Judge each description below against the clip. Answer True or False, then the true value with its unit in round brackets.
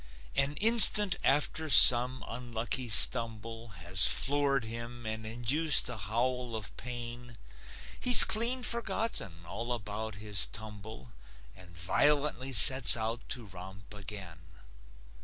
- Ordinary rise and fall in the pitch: True (4.3 semitones)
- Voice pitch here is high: False (115 Hz)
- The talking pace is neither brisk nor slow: False (115 wpm)